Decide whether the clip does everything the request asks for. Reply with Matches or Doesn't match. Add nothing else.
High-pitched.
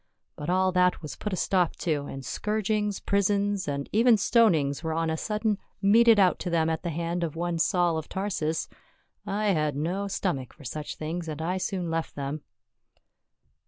Doesn't match